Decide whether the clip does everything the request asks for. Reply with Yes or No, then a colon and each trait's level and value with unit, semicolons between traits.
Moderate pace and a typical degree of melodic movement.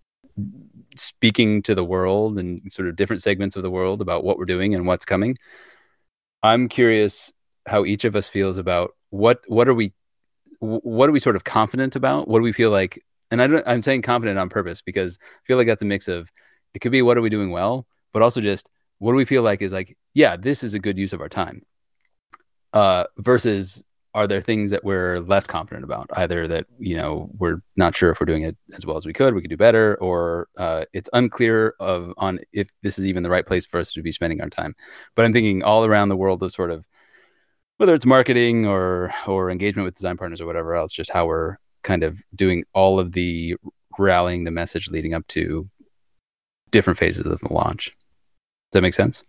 No: fast, 220 wpm; average, 3.8 semitones